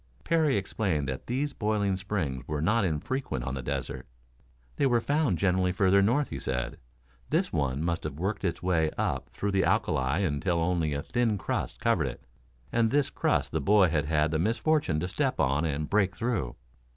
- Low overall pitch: Yes, very low, 95 Hz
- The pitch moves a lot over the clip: Yes, wide, 6.6 semitones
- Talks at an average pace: Yes, average, 190 wpm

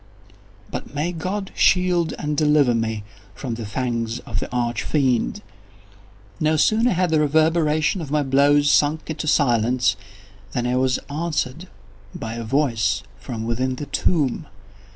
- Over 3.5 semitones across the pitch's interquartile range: Yes, average, 4.7 semitones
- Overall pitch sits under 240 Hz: Yes, medium, 140 Hz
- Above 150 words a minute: No, average, 145 wpm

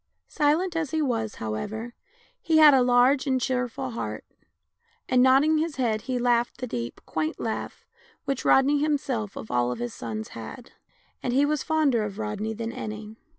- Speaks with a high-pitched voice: Yes, high, 245 Hz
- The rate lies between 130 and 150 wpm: No, average, 180 wpm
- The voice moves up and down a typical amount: Yes, average, 4.6 semitones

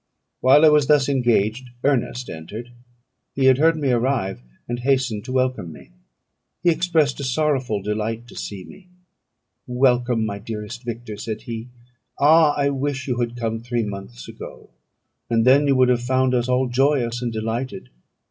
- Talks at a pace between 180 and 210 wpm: No, average, 165 wpm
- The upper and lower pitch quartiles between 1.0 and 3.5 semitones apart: Yes, average, 3.1 semitones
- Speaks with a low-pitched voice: Yes, low, 125 Hz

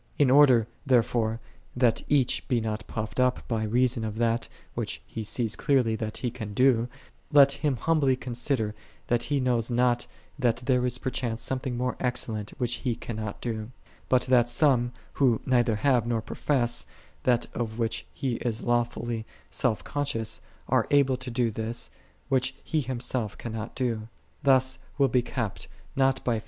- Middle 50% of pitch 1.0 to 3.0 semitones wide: Yes, narrow, 2.4 semitones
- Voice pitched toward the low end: Yes, low, 120 Hz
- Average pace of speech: Yes, average, 170 wpm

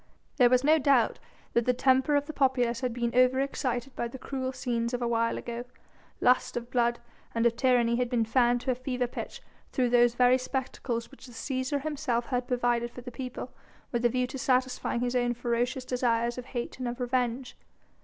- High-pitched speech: Yes, high, 245 Hz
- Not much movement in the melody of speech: Yes, narrow, 1.4 semitones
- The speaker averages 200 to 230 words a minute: Yes, fast, 205 wpm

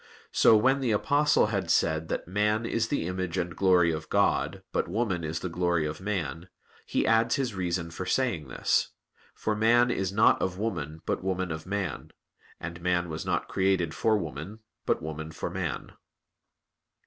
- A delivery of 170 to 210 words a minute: Yes, average, 175 wpm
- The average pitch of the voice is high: No, very low, 95 Hz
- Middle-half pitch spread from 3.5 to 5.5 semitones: Yes, average, 4.4 semitones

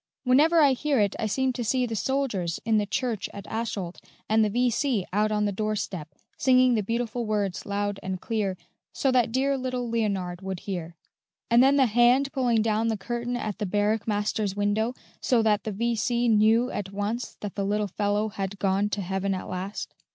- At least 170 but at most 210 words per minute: Yes, average, 200 wpm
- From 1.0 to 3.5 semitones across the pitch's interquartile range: Yes, average, 3.2 semitones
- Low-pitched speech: No, high, 215 Hz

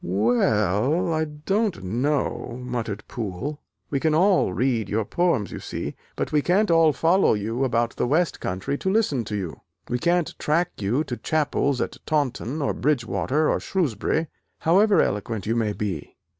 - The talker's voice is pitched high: No, low, 135 Hz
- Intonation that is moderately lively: No, wide, 6.6 semitones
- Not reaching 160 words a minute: No, average, 170 wpm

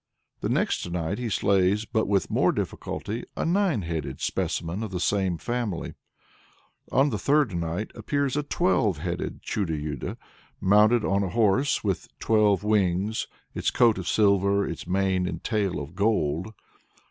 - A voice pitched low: Yes, low, 100 Hz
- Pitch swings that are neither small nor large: Yes, average, 3.7 semitones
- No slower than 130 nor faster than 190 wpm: Yes, average, 155 wpm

